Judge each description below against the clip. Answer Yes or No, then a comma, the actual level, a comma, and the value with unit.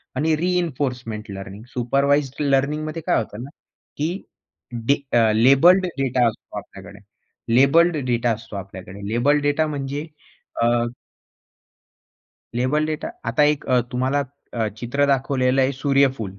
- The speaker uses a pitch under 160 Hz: Yes, low, 135 Hz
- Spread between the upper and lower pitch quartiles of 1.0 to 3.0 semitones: No, average, 3.6 semitones